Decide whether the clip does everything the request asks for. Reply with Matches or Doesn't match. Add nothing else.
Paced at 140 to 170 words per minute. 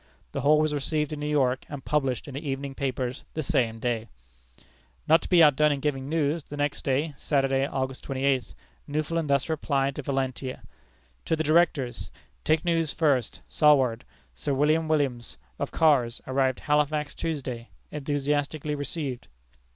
Matches